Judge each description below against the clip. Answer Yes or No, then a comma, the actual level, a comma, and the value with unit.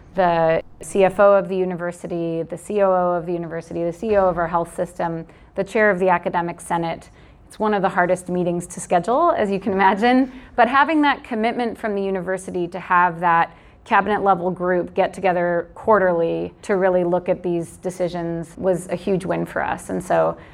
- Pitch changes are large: No, narrow, 2.4 semitones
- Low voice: No, medium, 180 Hz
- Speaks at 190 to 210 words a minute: No, average, 180 wpm